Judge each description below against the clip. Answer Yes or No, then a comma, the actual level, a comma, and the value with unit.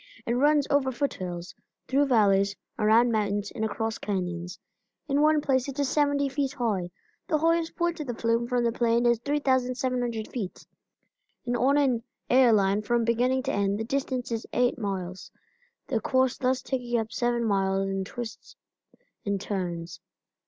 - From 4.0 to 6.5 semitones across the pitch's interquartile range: Yes, average, 4.3 semitones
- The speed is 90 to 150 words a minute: No, average, 165 wpm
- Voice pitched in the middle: No, high, 240 Hz